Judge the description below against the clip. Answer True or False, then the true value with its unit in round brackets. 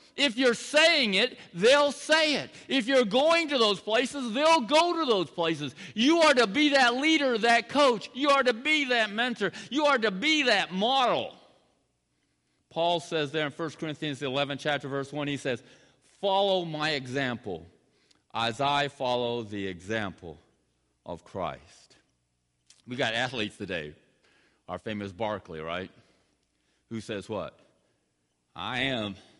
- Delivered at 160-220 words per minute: False (150 wpm)